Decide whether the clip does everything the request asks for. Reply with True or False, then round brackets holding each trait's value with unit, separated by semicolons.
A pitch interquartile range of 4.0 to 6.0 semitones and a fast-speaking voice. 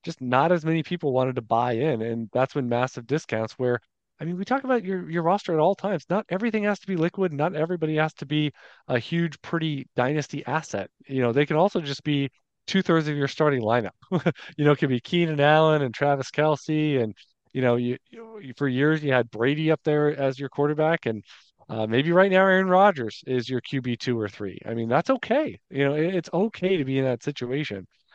True (4.9 semitones; 225 wpm)